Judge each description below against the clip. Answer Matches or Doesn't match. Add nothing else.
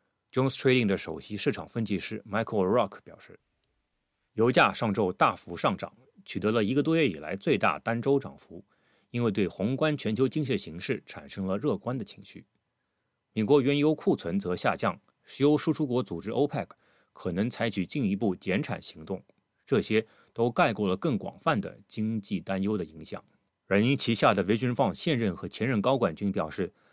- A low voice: Matches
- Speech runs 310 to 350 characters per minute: Matches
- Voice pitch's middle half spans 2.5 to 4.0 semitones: Doesn't match